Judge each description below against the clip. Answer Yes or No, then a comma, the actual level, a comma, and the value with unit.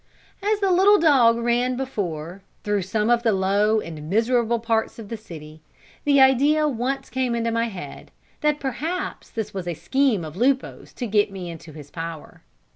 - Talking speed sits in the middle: Yes, average, 180 wpm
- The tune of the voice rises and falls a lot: Yes, wide, 5.8 semitones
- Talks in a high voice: Yes, high, 230 Hz